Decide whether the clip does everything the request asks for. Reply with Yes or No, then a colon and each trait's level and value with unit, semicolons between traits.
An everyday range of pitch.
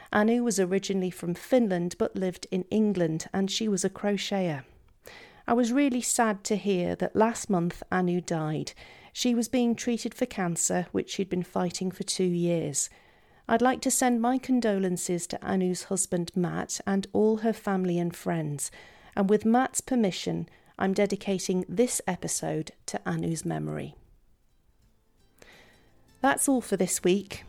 Yes: average, 4.2 semitones